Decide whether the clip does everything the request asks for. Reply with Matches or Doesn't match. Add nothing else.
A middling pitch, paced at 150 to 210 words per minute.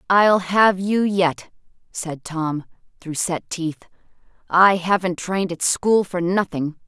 Doesn't match